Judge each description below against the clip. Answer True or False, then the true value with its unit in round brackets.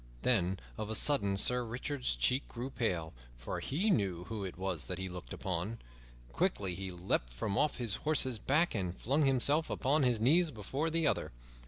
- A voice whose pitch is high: False (110 Hz)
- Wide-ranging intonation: True (6.8 semitones)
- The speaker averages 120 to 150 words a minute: False (185 wpm)